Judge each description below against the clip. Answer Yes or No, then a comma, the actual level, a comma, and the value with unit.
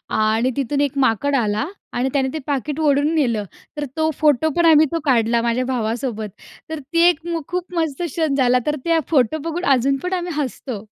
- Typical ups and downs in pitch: Yes, average, 4.5 semitones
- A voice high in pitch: Yes, very high, 280 Hz